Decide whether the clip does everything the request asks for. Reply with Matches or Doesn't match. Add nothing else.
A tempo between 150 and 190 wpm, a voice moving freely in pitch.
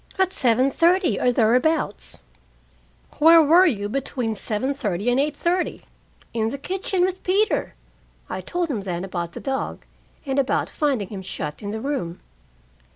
Matches